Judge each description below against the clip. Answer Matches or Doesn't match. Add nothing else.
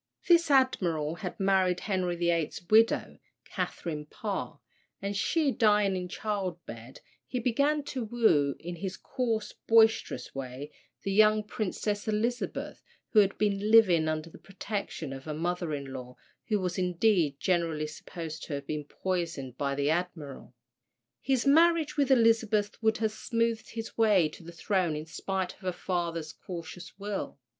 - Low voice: Doesn't match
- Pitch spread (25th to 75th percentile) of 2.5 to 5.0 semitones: Doesn't match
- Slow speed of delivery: Doesn't match